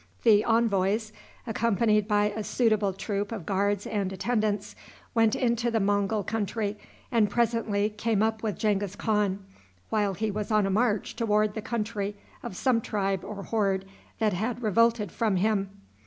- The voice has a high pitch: Yes, high, 210 Hz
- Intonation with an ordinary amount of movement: No, narrow, 1.9 semitones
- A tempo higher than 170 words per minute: No, average, 155 wpm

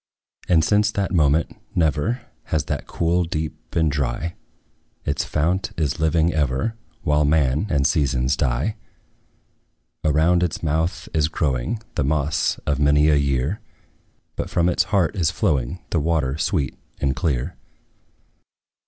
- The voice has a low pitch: Yes, very low, 80 Hz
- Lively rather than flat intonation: No, average, 3.2 semitones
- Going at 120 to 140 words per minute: Yes, slow, 135 wpm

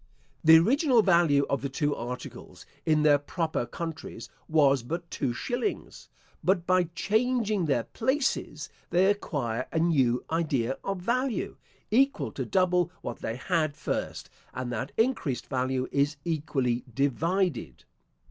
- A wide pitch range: Yes, wide, 6.2 semitones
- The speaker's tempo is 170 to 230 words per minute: No, slow, 135 wpm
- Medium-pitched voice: Yes, medium, 160 Hz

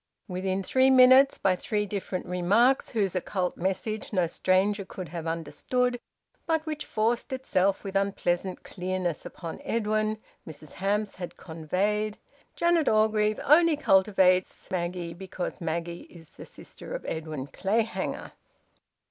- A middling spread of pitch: Yes, average, 3.4 semitones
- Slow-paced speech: Yes, slow, 130 wpm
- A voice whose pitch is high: Yes, high, 195 Hz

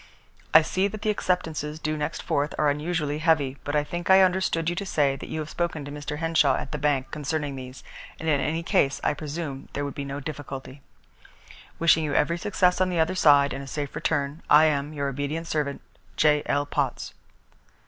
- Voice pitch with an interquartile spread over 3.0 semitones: No, narrow, 2.5 semitones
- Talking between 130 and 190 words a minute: No, fast, 205 wpm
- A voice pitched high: No, medium, 150 Hz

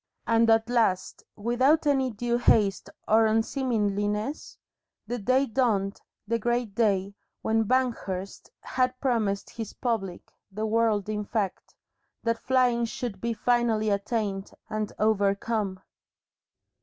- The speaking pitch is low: No, high, 225 Hz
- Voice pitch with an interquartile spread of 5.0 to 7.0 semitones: No, average, 2.8 semitones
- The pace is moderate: No, slow, 120 wpm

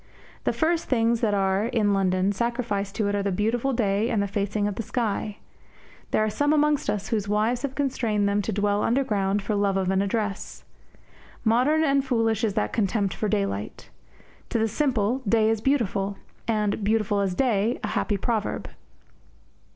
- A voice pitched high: Yes, high, 215 Hz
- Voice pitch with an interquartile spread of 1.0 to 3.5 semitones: Yes, average, 2.8 semitones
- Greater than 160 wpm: Yes, average, 180 wpm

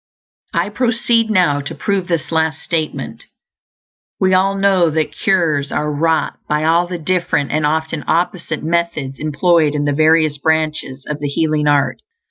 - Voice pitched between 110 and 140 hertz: No, medium, 160 Hz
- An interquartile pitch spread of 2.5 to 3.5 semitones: Yes, average, 2.9 semitones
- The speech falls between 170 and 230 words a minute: No, average, 155 wpm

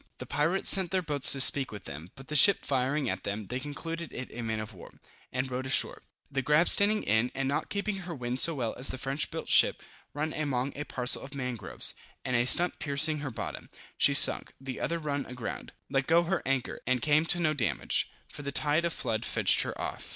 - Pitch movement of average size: Yes, average, 3.5 semitones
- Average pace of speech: No, fast, 225 wpm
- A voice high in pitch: No, medium, 140 Hz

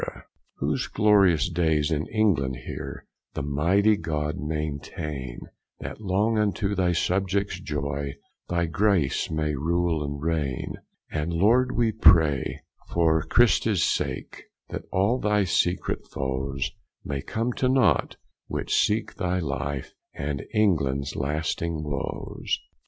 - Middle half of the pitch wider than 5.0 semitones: Yes, wide, 5.6 semitones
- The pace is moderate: No, slow, 120 wpm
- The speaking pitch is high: No, very low, 80 Hz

